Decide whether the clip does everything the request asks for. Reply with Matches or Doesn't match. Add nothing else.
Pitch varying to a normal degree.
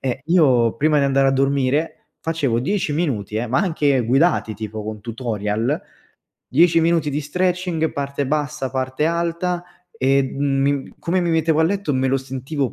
Matches